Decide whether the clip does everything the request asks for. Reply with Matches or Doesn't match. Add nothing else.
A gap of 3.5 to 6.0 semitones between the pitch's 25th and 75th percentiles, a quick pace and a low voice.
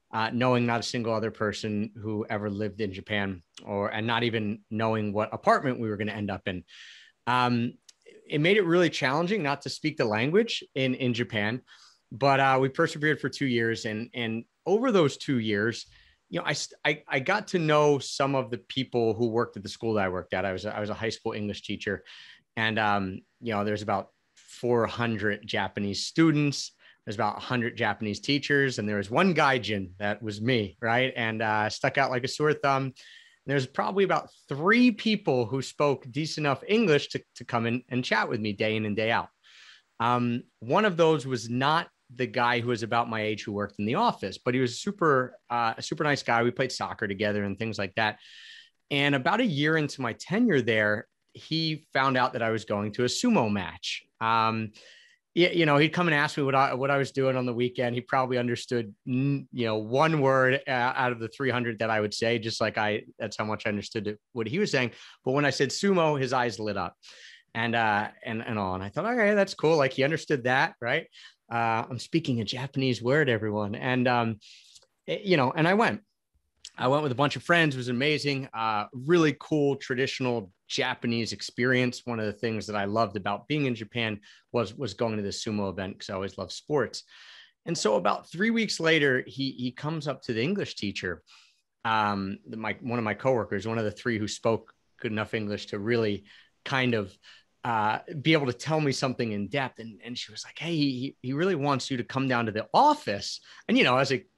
Matches